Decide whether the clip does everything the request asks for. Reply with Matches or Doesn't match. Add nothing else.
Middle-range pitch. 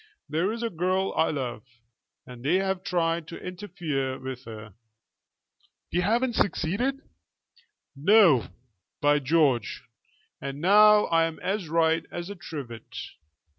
Matches